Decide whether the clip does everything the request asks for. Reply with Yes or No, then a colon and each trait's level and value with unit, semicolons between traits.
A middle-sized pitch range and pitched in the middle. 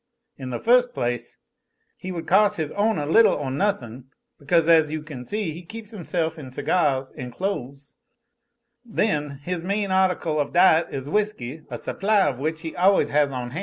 No: wide, 5.8 semitones; medium, 160 Hz